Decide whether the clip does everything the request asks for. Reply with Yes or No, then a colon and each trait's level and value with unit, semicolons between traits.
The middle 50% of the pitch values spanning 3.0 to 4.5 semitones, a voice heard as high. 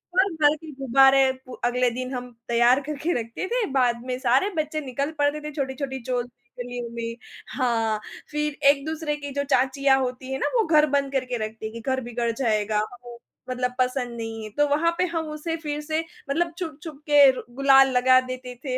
Yes: average, 3.3 semitones; very high, 265 Hz